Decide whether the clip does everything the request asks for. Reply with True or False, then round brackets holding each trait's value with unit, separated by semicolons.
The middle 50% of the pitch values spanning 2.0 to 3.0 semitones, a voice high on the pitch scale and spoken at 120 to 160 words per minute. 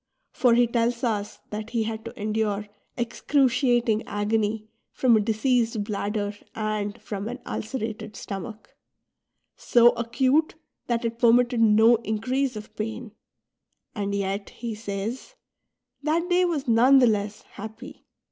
True (2.5 semitones; 225 Hz; 145 wpm)